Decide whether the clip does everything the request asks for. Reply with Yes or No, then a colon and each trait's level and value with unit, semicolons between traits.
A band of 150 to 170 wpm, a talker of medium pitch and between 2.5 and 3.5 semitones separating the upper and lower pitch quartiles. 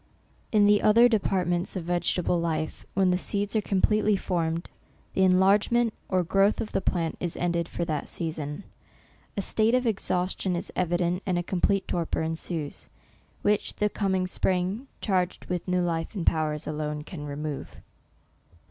Yes: average, 165 wpm; medium, 180 Hz; average, 3.1 semitones